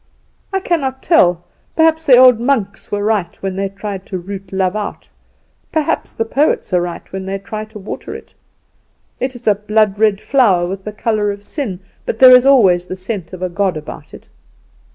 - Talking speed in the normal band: Yes, average, 195 wpm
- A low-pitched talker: No, high, 205 Hz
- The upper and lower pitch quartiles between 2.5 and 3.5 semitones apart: No, average, 4.6 semitones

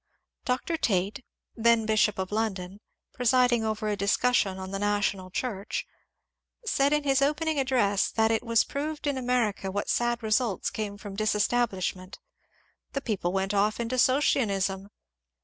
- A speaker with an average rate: Yes, average, 150 wpm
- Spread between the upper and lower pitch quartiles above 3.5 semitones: Yes, average, 4.0 semitones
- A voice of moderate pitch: No, high, 220 Hz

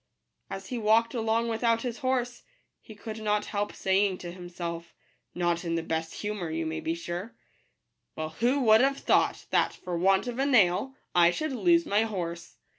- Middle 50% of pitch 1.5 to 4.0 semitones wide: No, average, 5.2 semitones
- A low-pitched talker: No, high, 205 Hz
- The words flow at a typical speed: Yes, average, 190 wpm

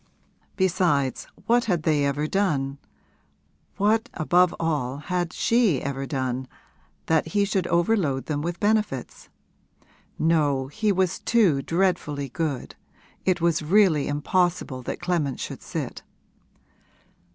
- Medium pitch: Yes, medium, 165 Hz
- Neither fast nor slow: No, slow, 120 wpm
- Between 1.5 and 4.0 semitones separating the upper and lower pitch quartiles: No, average, 4.9 semitones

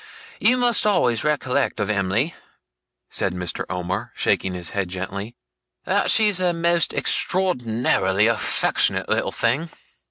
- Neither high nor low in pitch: No, low, 115 Hz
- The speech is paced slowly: Yes, slow, 125 wpm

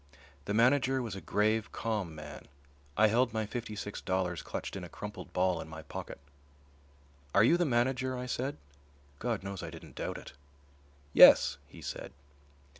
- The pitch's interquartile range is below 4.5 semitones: No, average, 4.8 semitones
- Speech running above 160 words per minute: Yes, average, 170 wpm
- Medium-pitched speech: No, low, 110 Hz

